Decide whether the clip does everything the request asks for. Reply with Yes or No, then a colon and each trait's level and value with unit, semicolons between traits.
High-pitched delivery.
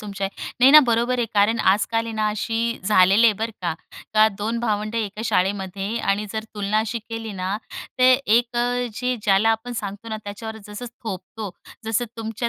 Yes: high, 220 Hz